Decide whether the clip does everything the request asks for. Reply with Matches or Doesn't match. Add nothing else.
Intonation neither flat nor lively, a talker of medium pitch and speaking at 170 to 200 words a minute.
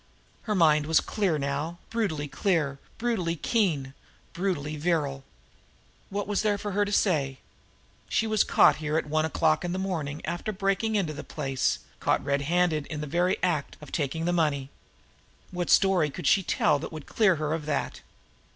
Matches